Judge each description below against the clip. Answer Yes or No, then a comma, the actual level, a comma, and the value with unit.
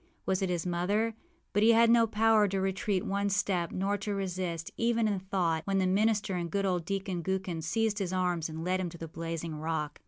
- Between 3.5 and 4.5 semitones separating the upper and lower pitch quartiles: No, average, 3.0 semitones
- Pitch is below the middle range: No, high, 190 Hz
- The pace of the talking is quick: Yes, fast, 220 wpm